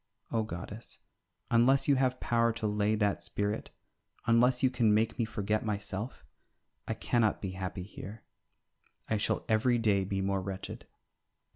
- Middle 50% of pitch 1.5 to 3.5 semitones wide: Yes, narrow, 2.5 semitones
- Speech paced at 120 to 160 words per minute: Yes, average, 150 wpm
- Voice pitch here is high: No, low, 110 Hz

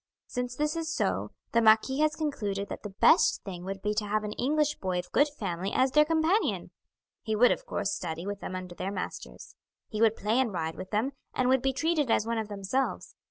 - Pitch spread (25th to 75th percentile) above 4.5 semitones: Yes, wide, 5.6 semitones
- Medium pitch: No, high, 220 Hz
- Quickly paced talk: Yes, fast, 225 wpm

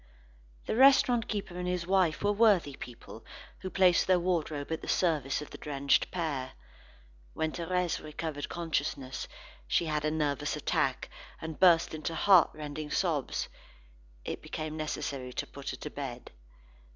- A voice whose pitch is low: No, medium, 160 Hz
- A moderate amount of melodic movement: Yes, average, 3.7 semitones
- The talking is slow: No, average, 150 wpm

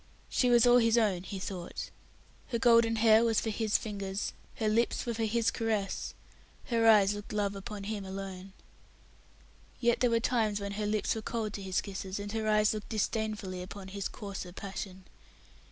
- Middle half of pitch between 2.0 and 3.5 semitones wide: Yes, narrow, 2.4 semitones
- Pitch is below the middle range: No, high, 210 Hz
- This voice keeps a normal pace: Yes, average, 185 wpm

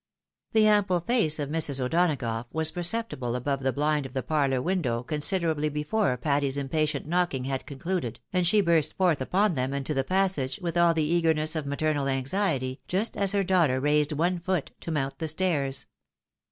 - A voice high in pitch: No, medium, 155 Hz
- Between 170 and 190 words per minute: Yes, average, 180 wpm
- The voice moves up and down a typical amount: Yes, average, 4.6 semitones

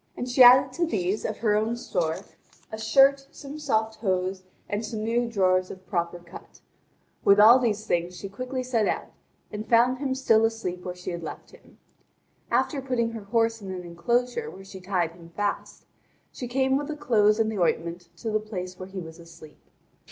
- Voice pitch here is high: Yes, high, 215 Hz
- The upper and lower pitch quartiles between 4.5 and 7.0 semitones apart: Yes, average, 5.0 semitones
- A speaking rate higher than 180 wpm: Yes, average, 195 wpm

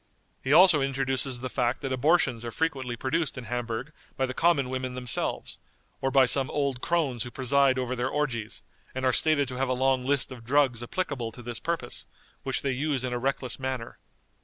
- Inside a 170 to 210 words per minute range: Yes, average, 200 wpm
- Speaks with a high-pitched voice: No, low, 130 Hz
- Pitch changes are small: Yes, narrow, 2.1 semitones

